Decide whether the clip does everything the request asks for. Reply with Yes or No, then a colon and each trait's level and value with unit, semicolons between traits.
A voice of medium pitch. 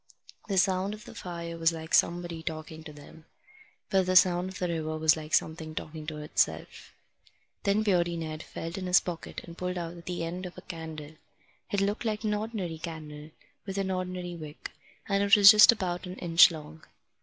Yes: medium, 175 Hz